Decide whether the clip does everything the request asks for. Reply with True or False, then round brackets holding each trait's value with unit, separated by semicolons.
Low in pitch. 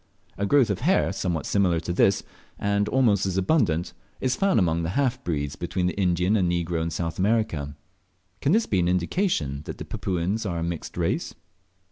True (90 Hz)